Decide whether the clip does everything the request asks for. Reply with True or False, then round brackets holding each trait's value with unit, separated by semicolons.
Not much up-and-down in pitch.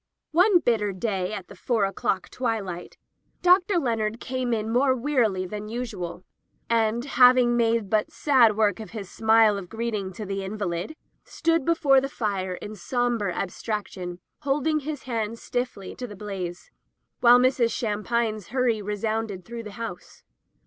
False (3.7 semitones)